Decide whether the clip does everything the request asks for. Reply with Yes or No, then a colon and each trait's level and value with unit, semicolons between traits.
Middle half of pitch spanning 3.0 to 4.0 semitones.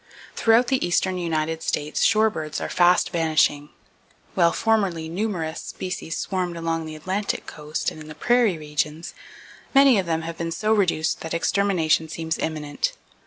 Yes: average, 3.6 semitones